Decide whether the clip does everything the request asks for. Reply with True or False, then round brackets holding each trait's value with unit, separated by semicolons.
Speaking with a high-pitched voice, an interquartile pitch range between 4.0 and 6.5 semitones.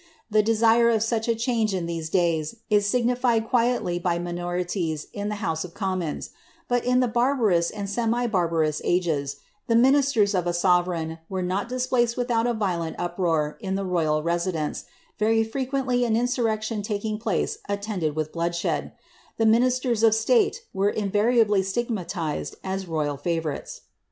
True (205 Hz; 5.1 semitones)